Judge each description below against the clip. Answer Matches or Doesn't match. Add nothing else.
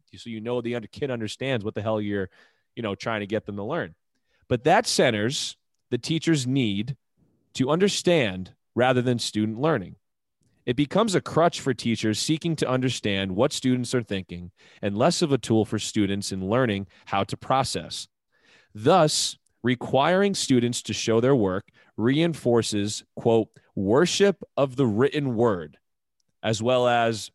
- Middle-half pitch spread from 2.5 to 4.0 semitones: Doesn't match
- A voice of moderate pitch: Doesn't match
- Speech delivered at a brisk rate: Doesn't match